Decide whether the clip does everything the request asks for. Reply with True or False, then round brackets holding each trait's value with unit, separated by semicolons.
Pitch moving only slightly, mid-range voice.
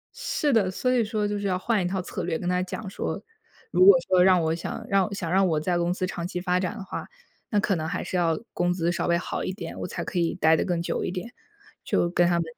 True (2.2 semitones; 180 Hz)